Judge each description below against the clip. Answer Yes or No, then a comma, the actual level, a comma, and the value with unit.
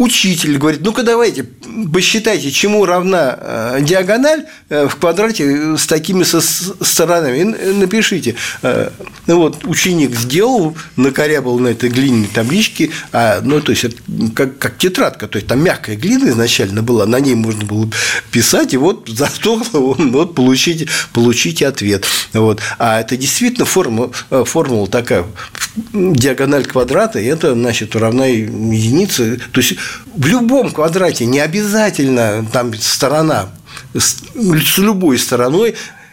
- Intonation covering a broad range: Yes, wide, 7.2 semitones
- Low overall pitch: No, medium, 145 Hz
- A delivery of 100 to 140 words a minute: Yes, average, 130 wpm